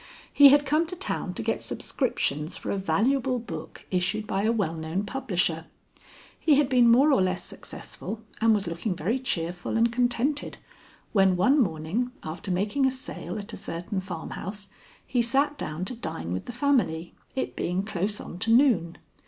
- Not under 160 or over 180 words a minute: Yes, average, 175 wpm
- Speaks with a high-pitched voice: Yes, high, 215 Hz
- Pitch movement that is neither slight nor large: No, wide, 6.4 semitones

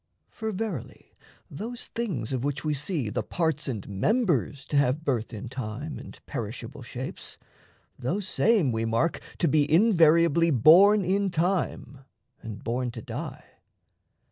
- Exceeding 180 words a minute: No, average, 145 wpm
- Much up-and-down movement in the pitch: Yes, wide, 6.8 semitones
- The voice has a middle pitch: Yes, medium, 150 Hz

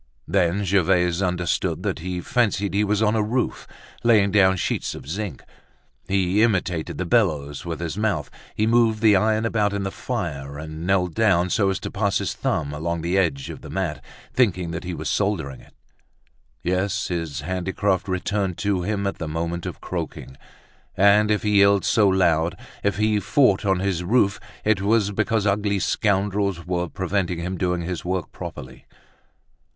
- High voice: No, very low, 95 Hz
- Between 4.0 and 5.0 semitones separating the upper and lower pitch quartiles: No, average, 3.0 semitones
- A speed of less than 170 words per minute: No, average, 175 wpm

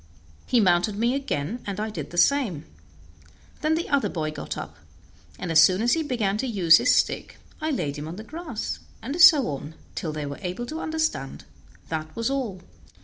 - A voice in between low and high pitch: No, high, 210 Hz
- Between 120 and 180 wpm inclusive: No, average, 200 wpm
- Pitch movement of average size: No, wide, 8.9 semitones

